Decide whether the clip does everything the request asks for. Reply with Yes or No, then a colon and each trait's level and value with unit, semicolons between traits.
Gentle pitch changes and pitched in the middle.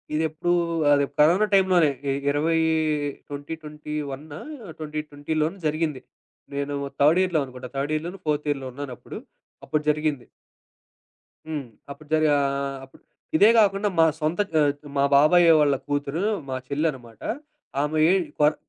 Yes: narrow, 2.1 semitones; medium, 150 Hz